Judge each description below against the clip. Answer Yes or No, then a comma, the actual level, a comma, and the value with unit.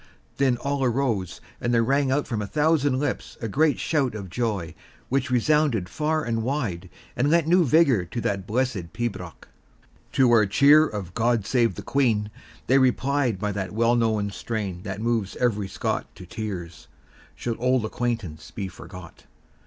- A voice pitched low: Yes, low, 115 Hz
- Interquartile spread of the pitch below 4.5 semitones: No, average, 5.1 semitones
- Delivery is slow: No, average, 170 wpm